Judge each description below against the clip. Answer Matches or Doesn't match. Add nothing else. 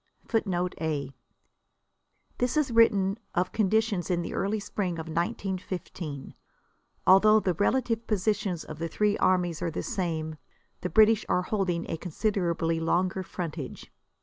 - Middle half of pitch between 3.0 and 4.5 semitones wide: Matches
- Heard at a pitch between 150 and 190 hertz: Matches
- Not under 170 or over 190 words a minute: Doesn't match